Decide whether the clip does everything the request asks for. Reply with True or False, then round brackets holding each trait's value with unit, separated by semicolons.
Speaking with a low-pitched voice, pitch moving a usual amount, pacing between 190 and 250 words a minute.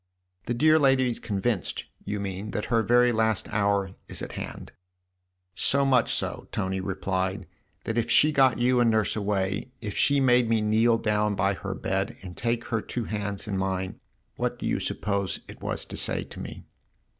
True (105 Hz; 3.8 semitones; 200 wpm)